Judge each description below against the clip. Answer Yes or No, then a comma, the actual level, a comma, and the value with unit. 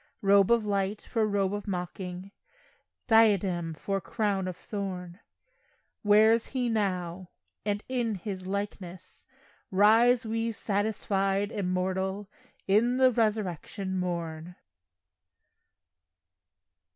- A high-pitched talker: Yes, high, 200 Hz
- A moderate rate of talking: No, slow, 95 wpm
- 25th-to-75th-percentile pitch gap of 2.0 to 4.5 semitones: Yes, average, 2.9 semitones